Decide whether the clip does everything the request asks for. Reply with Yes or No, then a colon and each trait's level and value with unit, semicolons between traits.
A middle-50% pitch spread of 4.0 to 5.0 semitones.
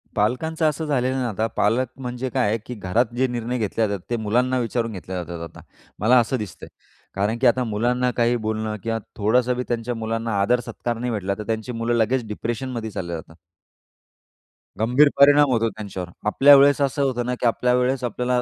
No: narrow, 2.6 semitones